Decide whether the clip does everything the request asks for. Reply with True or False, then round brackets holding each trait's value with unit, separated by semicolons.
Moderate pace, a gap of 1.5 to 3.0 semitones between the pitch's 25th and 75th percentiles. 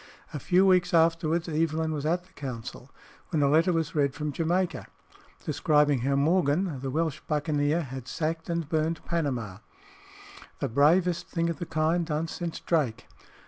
True (160 wpm; 2.7 semitones)